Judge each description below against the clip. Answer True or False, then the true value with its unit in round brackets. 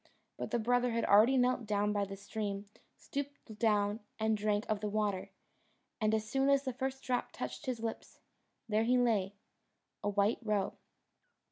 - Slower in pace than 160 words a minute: False (170 wpm)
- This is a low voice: False (220 Hz)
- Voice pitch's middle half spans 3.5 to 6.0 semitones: False (3.1 semitones)